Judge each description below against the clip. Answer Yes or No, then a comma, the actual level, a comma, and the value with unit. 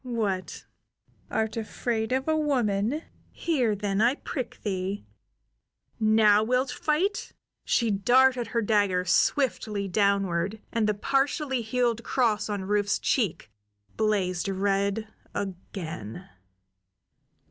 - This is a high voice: Yes, high, 215 Hz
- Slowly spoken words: Yes, slow, 105 wpm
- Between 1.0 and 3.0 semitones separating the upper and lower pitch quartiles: No, average, 3.9 semitones